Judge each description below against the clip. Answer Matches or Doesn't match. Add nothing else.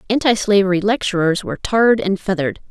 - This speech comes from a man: Doesn't match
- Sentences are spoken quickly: Doesn't match